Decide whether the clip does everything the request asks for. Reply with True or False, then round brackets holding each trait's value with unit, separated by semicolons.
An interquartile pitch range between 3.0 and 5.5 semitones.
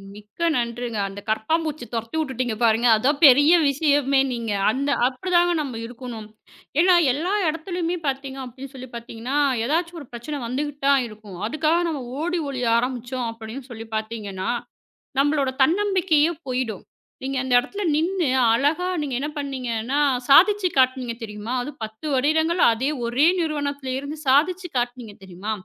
True (4.7 semitones)